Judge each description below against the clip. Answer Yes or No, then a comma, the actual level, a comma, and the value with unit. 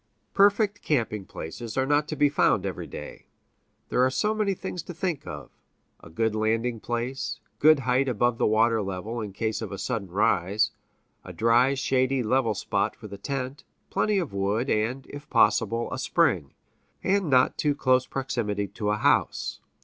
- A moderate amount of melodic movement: Yes, average, 4.3 semitones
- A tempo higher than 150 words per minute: Yes, average, 175 wpm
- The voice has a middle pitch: No, low, 120 Hz